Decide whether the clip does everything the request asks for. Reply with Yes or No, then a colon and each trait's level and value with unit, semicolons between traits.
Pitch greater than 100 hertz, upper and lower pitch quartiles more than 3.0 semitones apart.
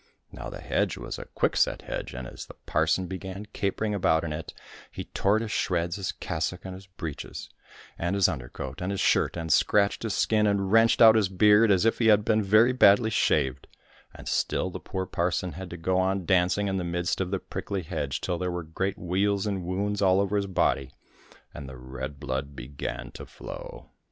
No: very low, 95 Hz; average, 3.5 semitones